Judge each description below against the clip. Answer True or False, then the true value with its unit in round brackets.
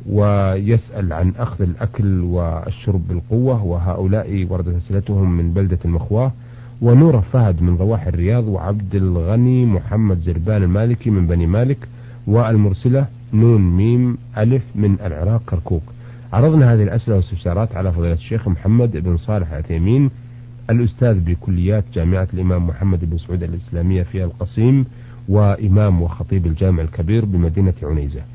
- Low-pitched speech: True (100 Hz)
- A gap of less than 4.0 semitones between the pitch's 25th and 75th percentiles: False (4.6 semitones)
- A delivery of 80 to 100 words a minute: False (125 wpm)